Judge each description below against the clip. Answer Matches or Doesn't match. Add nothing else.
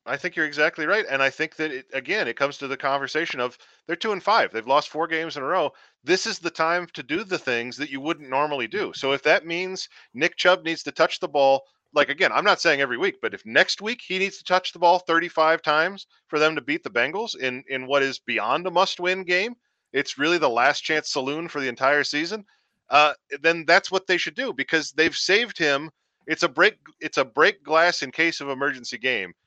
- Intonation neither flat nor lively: Matches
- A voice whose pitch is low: Doesn't match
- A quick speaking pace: Matches